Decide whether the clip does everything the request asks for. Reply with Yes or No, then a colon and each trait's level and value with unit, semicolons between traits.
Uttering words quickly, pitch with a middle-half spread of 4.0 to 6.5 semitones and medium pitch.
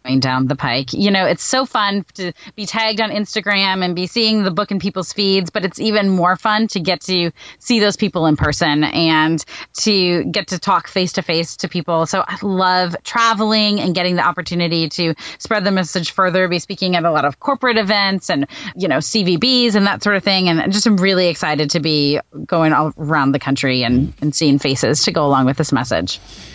Yes: fast, 220 wpm; average, 4.6 semitones; medium, 180 Hz